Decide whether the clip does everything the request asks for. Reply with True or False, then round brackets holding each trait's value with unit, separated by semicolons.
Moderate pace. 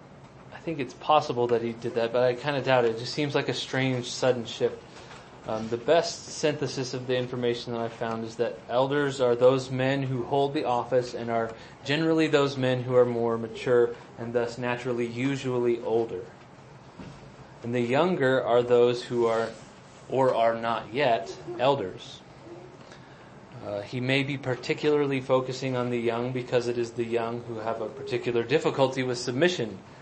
True (180 wpm)